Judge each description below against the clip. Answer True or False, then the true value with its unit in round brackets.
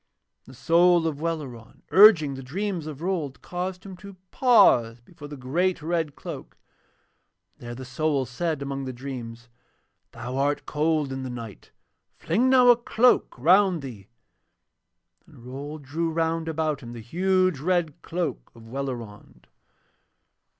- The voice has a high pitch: False (150 Hz)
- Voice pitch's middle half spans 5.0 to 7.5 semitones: True (5.3 semitones)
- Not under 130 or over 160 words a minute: True (150 wpm)